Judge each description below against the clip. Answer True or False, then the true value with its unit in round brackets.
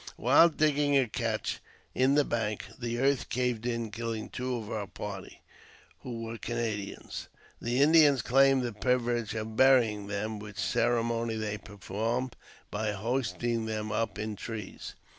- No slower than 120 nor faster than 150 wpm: True (145 wpm)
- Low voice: True (115 Hz)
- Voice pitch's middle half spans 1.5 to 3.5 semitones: True (2.8 semitones)